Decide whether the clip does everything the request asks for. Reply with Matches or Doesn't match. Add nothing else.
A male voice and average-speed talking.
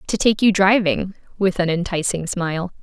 Doesn't match